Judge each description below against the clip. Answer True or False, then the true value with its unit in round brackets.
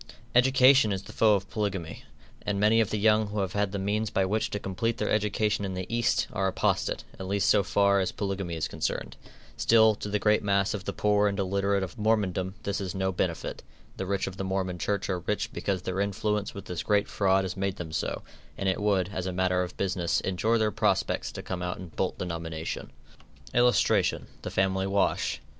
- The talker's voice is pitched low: True (100 Hz)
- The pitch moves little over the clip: True (1.9 semitones)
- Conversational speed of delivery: False (215 wpm)